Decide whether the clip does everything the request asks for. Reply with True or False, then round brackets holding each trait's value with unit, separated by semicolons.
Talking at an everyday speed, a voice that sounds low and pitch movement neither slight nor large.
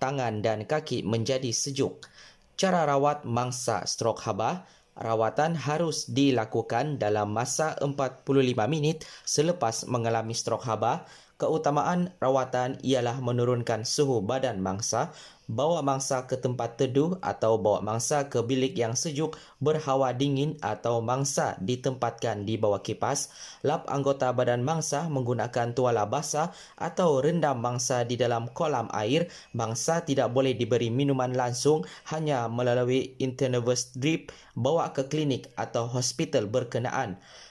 True (125 wpm; 130 Hz; 3.1 semitones)